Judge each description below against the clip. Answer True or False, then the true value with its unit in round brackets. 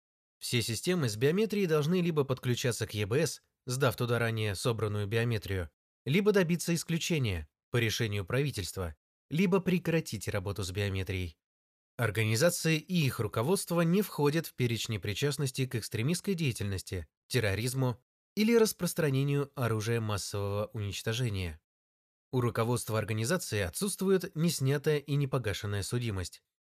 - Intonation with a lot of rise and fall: True (7.0 semitones)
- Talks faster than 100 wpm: True (115 wpm)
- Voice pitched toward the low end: True (120 Hz)